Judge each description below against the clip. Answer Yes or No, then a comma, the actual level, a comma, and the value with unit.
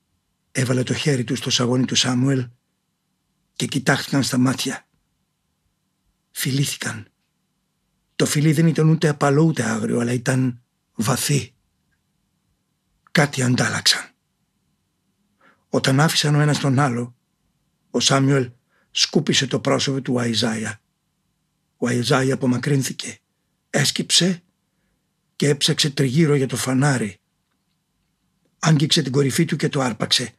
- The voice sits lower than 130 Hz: No, low, 135 Hz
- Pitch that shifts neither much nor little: Yes, average, 3.8 semitones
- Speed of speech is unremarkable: No, slow, 110 wpm